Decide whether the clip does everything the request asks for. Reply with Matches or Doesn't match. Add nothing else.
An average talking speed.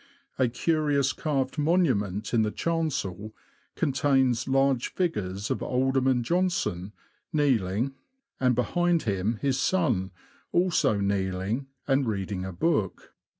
Doesn't match